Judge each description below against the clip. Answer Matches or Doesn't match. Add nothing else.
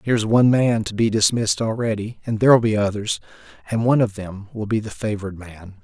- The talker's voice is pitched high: Doesn't match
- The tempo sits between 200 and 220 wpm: Matches